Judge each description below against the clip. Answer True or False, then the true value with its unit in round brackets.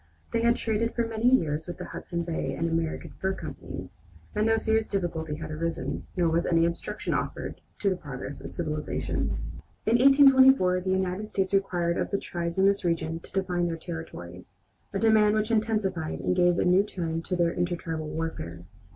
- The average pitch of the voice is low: False (180 Hz)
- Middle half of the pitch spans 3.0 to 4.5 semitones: True (4.2 semitones)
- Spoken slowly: False (185 wpm)